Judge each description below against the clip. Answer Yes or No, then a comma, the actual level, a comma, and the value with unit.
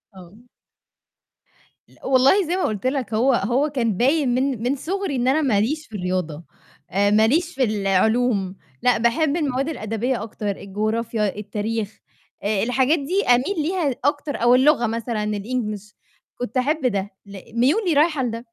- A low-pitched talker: No, high, 245 Hz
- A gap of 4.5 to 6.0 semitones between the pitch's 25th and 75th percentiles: Yes, average, 4.9 semitones